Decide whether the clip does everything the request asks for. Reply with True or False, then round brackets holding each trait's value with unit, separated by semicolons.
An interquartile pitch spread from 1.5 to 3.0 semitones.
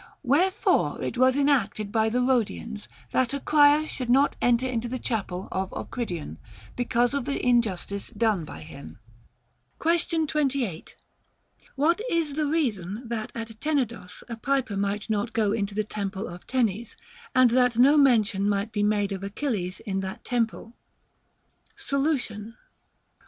False (4.7 semitones)